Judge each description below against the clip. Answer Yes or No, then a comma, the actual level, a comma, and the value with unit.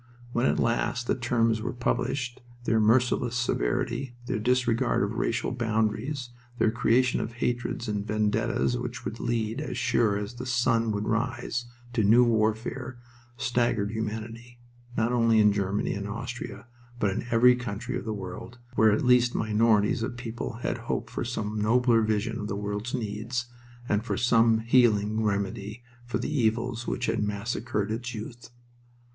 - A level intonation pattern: Yes, narrow, 2.1 semitones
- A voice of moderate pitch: No, low, 115 Hz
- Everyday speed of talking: Yes, average, 160 wpm